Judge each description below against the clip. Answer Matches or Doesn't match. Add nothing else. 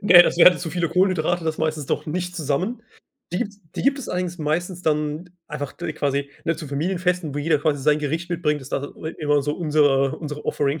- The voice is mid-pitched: Matches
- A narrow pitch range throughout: Doesn't match